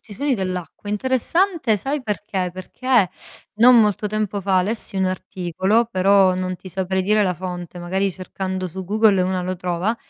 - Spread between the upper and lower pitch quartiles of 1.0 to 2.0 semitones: No, narrow, 2.6 semitones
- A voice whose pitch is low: No, high, 190 Hz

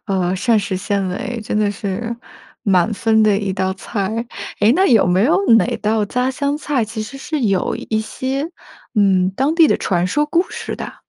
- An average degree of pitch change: Yes, average, 4.8 semitones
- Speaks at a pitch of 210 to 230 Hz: Yes, high, 215 Hz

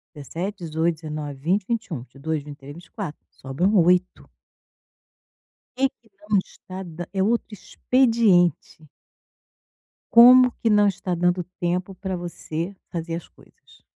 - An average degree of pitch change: Yes, average, 4.0 semitones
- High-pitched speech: No, medium, 175 Hz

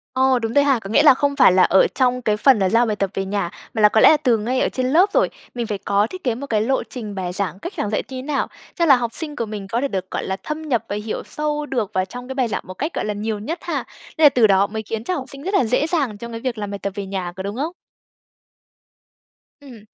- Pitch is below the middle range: No, high, 230 Hz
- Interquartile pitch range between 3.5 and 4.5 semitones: No, average, 5.0 semitones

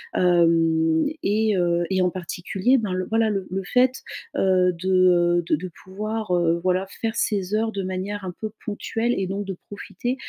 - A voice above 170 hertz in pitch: Yes, high, 190 Hz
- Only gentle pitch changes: No, average, 3.0 semitones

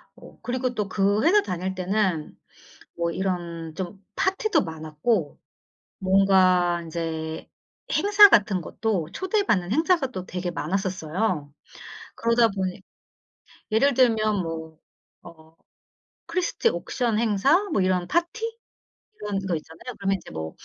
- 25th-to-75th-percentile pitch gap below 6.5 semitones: Yes, wide, 5.4 semitones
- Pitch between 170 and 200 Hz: Yes, high, 190 Hz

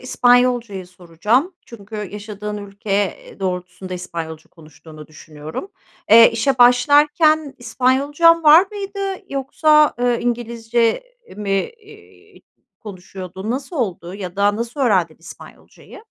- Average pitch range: No, wide, 6.4 semitones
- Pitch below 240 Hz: Yes, high, 230 Hz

